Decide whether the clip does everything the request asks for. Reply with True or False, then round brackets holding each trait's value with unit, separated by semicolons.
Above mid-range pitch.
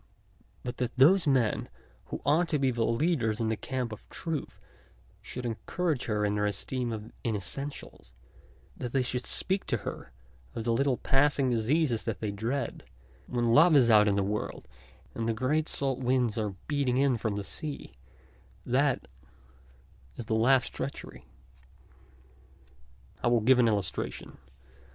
False (125 Hz)